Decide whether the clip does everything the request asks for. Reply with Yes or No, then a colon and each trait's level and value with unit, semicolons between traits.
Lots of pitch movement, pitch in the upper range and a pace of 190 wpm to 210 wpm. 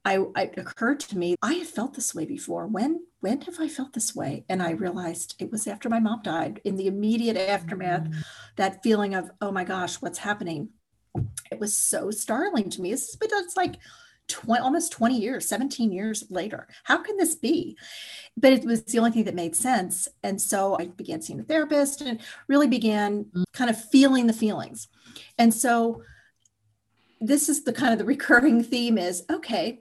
Yes: wide, 5.9 semitones; high, 225 Hz; average, 195 wpm